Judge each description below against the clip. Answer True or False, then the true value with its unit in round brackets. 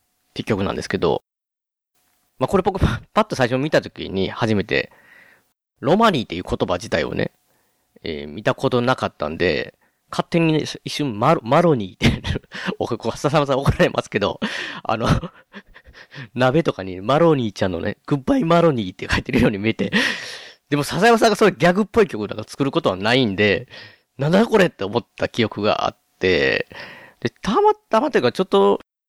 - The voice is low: False (145 Hz)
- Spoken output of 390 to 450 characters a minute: False (355 characters per minute)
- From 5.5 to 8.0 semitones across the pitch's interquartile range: False (8.5 semitones)